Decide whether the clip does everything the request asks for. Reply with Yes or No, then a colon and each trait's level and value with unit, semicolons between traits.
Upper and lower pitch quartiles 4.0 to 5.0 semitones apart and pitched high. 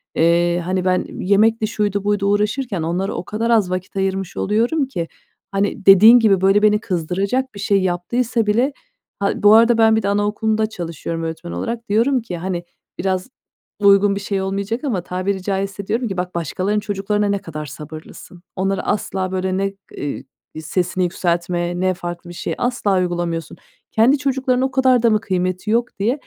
No: average, 3.4 semitones; high, 195 Hz